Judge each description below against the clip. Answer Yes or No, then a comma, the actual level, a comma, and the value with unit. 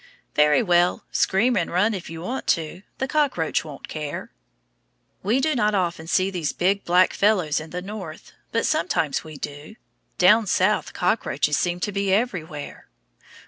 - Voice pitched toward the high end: No, medium, 180 Hz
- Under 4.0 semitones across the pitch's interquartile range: No, average, 4.6 semitones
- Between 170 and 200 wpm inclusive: No, average, 160 wpm